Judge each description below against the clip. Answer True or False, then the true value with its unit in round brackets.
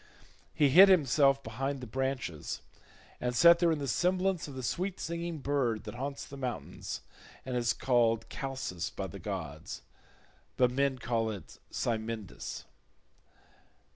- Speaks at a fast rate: False (140 wpm)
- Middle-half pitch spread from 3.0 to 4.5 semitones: True (3.7 semitones)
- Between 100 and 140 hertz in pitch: True (135 Hz)